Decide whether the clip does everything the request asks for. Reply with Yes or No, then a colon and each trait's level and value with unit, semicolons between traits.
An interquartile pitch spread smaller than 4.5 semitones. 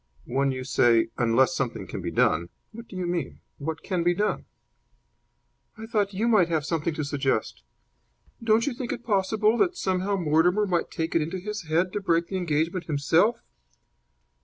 No: average, 5.3 semitones